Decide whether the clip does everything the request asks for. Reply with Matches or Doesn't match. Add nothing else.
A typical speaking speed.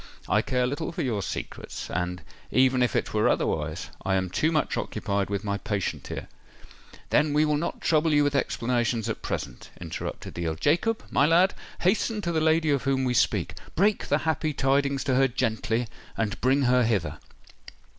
Matches